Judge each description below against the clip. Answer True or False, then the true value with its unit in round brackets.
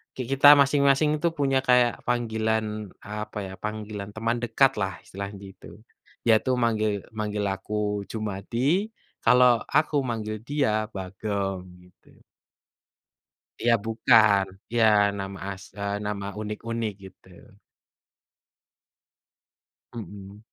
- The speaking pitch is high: False (110 Hz)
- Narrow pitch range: False (3.0 semitones)